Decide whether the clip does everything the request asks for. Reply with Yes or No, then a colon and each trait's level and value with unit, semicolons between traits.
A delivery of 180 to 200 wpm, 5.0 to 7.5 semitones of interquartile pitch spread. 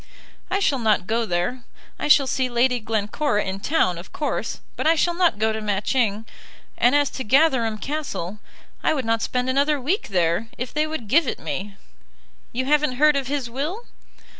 Yes: average, 190 wpm; wide, 5.5 semitones